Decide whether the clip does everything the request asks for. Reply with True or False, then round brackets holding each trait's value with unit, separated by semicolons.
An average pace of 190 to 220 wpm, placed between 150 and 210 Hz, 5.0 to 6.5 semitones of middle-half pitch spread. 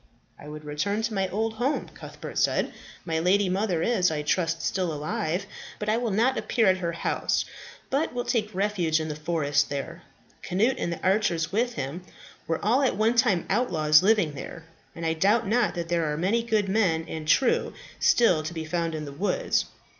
True (200 wpm; 185 Hz; 5.3 semitones)